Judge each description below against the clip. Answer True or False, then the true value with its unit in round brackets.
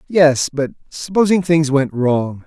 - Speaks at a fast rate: False (145 wpm)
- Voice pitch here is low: False (150 Hz)